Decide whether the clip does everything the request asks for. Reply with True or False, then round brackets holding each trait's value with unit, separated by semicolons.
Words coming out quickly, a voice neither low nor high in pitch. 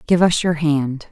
True (215 wpm; 155 Hz)